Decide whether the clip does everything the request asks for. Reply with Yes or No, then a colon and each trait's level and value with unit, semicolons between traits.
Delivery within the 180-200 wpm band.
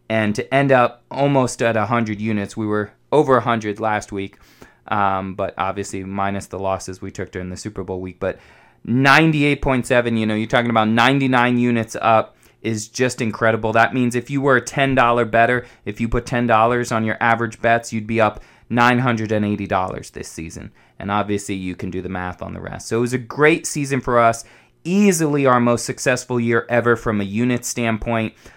Yes: average, 190 wpm